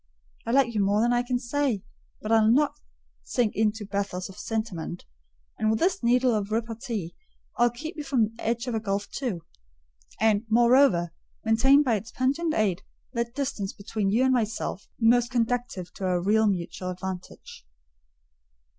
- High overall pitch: Yes, high, 225 Hz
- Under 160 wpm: No, average, 170 wpm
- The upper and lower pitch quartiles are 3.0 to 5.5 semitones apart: Yes, average, 3.5 semitones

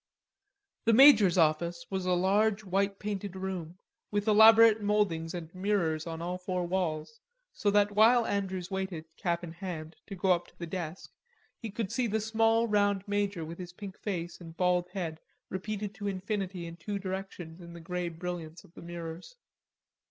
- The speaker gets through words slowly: No, average, 175 wpm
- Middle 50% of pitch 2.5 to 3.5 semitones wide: Yes, average, 3.2 semitones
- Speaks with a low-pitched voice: No, medium, 185 Hz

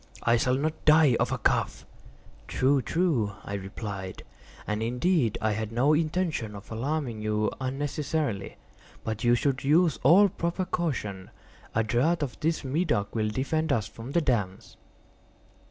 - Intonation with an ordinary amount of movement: No, wide, 6.3 semitones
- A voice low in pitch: Yes, low, 130 Hz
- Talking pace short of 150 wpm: Yes, average, 140 wpm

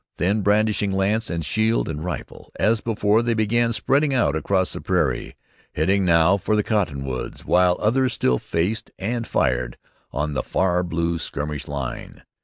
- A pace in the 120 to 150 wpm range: No, average, 160 wpm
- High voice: No, very low, 95 Hz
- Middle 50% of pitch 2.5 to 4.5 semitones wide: No, wide, 5.6 semitones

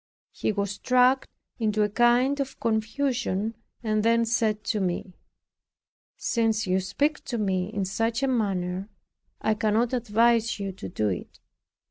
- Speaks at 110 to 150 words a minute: Yes, average, 140 wpm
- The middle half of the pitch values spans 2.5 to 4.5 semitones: Yes, average, 3.1 semitones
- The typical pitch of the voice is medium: No, high, 220 Hz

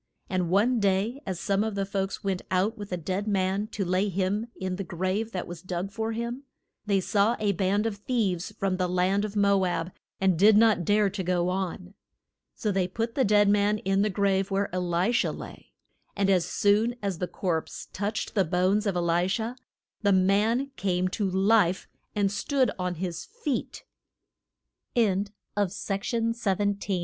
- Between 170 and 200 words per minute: Yes, average, 175 wpm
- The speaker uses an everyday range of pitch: No, narrow, 2.3 semitones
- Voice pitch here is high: Yes, high, 195 Hz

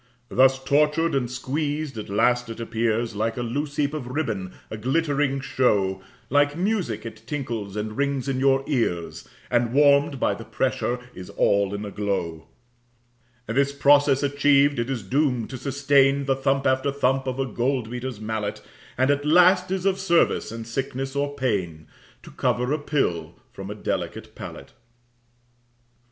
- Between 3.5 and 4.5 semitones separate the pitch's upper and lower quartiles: Yes, average, 4.0 semitones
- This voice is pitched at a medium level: No, low, 130 Hz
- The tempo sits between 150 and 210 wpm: Yes, average, 165 wpm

